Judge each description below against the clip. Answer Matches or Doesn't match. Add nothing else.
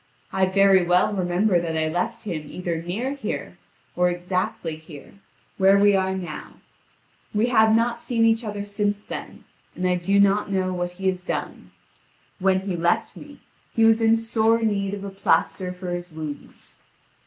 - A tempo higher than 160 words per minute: Matches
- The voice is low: Doesn't match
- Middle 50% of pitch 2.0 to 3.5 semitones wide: Matches